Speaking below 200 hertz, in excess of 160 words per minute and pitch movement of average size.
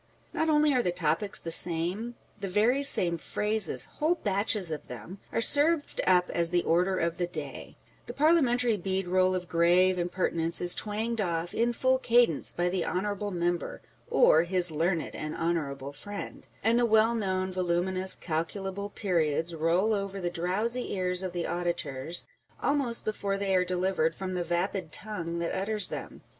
Yes: medium, 185 Hz; average, 175 wpm; average, 3.5 semitones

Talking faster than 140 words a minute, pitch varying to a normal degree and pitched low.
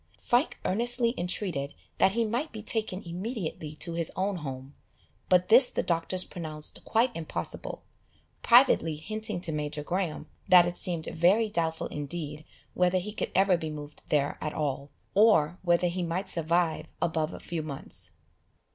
No: average, 155 wpm; average, 4.2 semitones; medium, 175 Hz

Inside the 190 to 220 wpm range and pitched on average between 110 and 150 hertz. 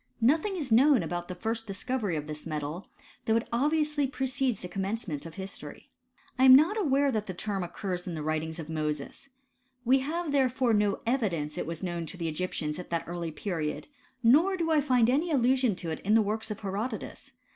No: fast, 205 wpm; high, 215 Hz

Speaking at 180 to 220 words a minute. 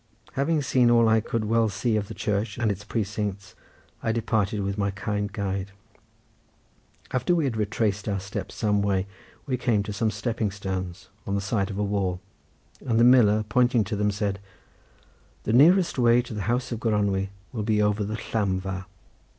Yes: average, 185 wpm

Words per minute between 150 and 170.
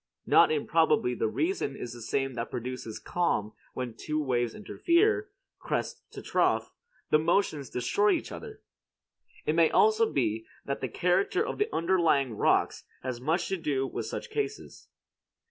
Yes: average, 155 wpm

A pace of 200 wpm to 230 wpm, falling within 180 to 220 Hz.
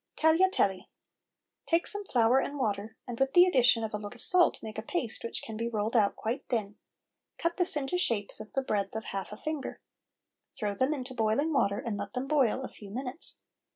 No: fast, 205 wpm; high, 240 Hz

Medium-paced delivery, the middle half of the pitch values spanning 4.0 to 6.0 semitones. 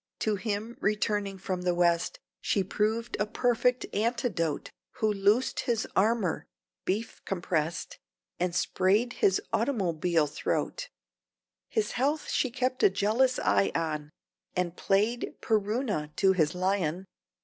No: slow, 125 wpm; average, 4.5 semitones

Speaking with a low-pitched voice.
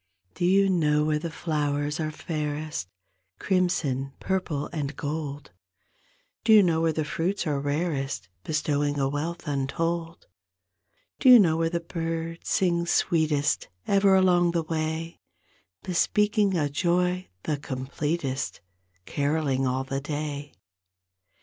No: medium, 160 Hz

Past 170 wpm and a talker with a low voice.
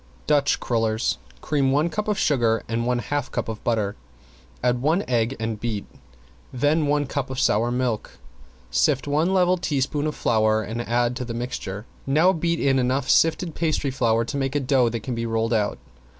Yes: average, 190 wpm; low, 125 Hz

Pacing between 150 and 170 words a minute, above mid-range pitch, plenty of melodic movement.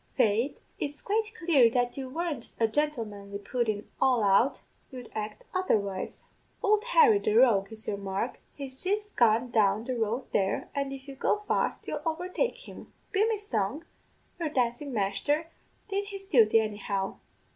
Yes: average, 165 wpm; very high, 255 Hz; wide, 7.5 semitones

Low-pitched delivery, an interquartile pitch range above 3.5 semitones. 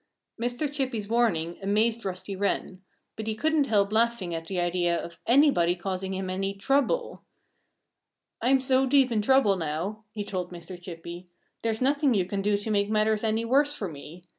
No: high, 205 Hz; average, 4.7 semitones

